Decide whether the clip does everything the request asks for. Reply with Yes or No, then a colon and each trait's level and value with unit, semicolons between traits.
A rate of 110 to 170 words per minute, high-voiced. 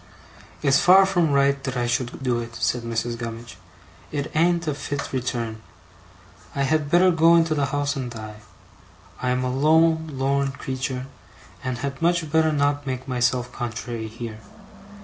No: average, 165 wpm; low, 135 Hz